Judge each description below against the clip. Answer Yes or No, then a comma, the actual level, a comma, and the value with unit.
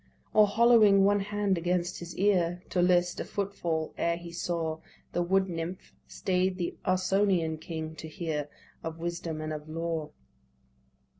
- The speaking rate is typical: Yes, average, 155 wpm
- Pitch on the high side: No, medium, 175 Hz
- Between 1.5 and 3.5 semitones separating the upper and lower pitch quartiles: Yes, average, 2.7 semitones